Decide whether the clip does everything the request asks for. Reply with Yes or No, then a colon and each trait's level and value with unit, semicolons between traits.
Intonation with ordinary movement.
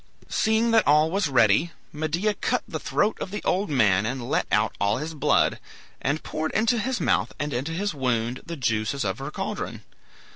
No: wide, 7.9 semitones